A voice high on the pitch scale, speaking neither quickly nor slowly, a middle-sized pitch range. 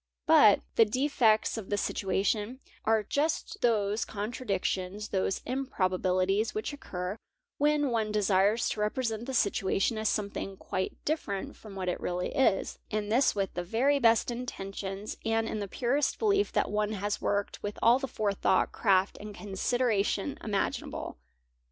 Yes: high, 210 Hz; average, 155 wpm; average, 3.5 semitones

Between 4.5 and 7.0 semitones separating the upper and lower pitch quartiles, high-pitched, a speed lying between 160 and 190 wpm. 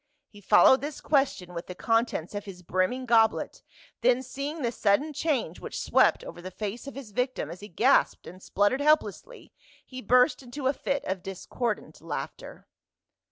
Yes: wide, 5.5 semitones; high, 240 Hz; average, 175 wpm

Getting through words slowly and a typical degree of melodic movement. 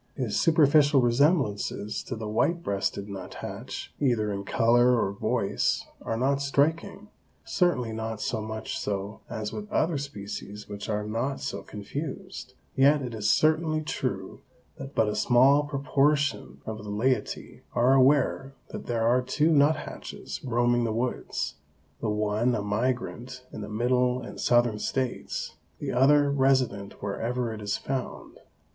No: average, 145 wpm; average, 4.6 semitones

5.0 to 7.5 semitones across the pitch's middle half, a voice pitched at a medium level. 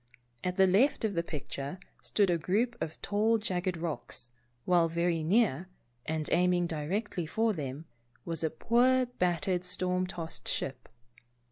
No: average, 3.9 semitones; medium, 180 Hz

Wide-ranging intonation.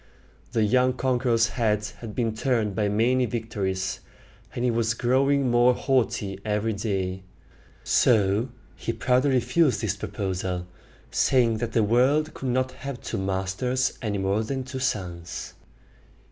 No: average, 3.9 semitones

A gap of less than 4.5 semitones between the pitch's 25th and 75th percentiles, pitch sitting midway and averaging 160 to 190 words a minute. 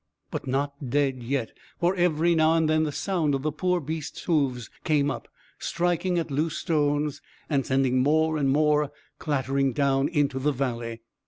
Yes: average, 2.7 semitones; medium, 145 Hz; average, 170 wpm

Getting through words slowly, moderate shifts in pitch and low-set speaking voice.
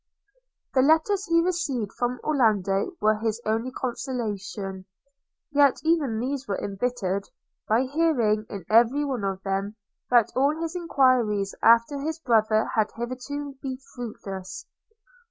No: slow, 130 wpm; average, 5.0 semitones; high, 240 Hz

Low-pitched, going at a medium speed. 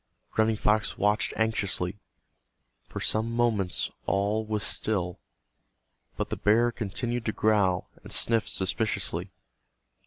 No: low, 110 Hz; slow, 115 wpm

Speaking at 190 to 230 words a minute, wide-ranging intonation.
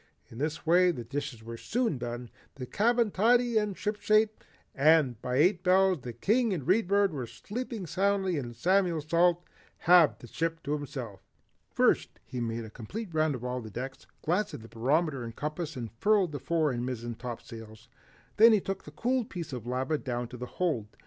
Yes: average, 195 wpm; wide, 7.6 semitones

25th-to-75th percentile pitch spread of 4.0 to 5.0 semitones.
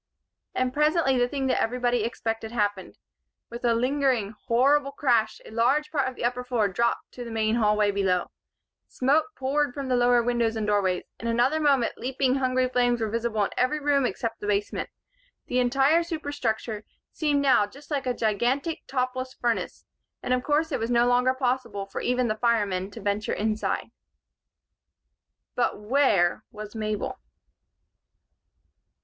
No: average, 3.4 semitones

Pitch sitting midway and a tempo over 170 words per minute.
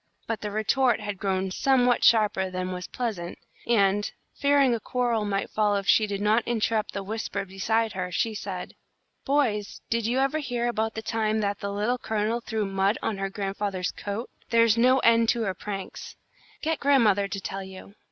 No: high, 215 Hz; average, 185 wpm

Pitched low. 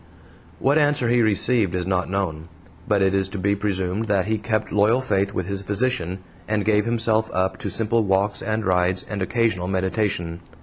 Yes: low, 100 Hz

